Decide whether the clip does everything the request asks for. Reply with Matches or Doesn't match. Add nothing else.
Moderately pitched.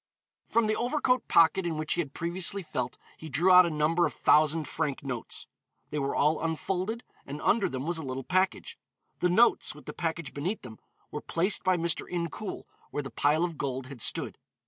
Matches